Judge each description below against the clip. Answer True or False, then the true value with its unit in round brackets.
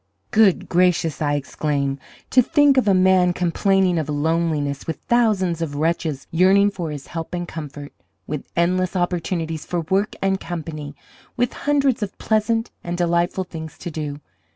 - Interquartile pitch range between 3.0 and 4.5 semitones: True (3.6 semitones)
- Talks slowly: False (155 wpm)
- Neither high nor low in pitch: True (175 Hz)